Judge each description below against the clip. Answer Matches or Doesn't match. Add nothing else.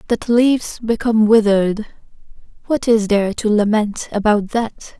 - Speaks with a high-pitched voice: Matches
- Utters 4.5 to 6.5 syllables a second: Matches